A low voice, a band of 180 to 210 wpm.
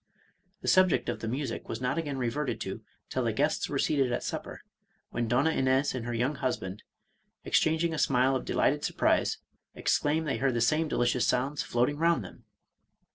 Yes: low, 130 Hz; average, 185 wpm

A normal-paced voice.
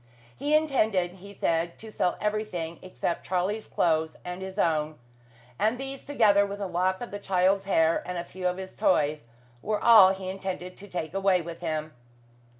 Yes: average, 180 wpm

